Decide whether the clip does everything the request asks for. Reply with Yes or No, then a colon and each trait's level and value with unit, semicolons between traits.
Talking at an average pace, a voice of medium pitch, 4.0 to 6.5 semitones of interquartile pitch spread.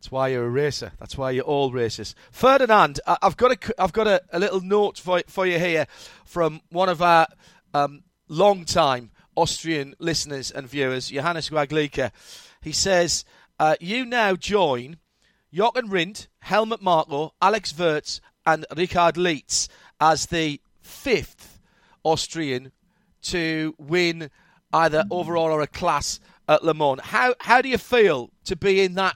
Yes: average, 150 wpm; medium, 165 Hz; average, 4.3 semitones